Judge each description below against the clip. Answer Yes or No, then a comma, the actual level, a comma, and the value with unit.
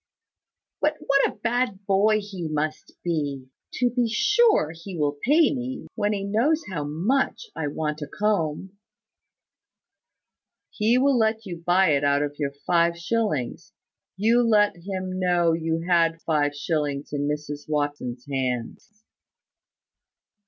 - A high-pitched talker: No, medium, 175 Hz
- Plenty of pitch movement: Yes, wide, 6.5 semitones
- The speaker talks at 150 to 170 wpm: No, average, 140 wpm